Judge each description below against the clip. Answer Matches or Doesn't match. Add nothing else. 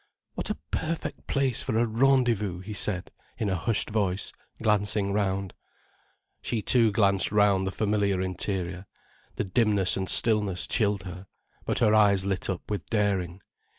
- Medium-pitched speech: Doesn't match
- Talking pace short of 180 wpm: Matches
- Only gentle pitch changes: Matches